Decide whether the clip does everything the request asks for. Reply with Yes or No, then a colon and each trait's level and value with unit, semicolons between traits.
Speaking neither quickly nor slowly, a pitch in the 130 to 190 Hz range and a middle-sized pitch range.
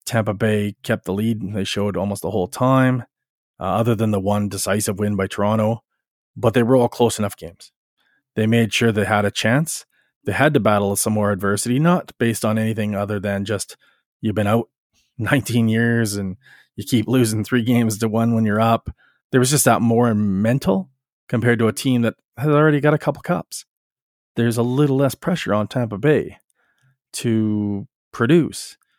No: average, 190 wpm; low, 115 Hz; average, 3.1 semitones